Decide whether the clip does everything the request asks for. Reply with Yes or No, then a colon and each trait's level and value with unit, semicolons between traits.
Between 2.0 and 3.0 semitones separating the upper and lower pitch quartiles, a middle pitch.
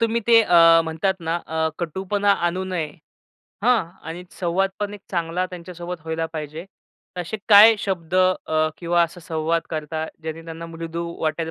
Yes: narrow, 2.5 semitones; medium, 170 Hz